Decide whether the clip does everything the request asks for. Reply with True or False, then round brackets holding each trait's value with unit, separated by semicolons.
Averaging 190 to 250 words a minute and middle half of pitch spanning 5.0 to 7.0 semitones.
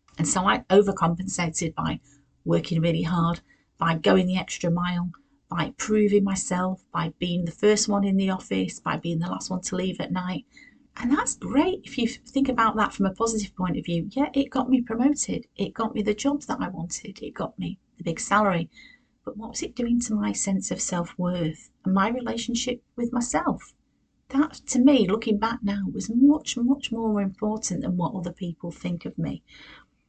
True (200 wpm; 5.4 semitones)